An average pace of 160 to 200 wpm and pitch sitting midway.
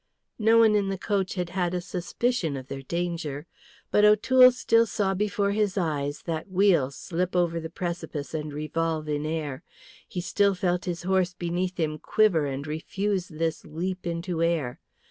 Yes: average, 170 wpm; medium, 175 Hz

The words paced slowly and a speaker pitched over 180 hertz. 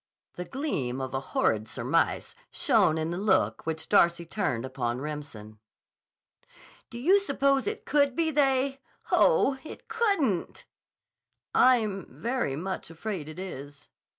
Yes: slow, 130 wpm; high, 190 Hz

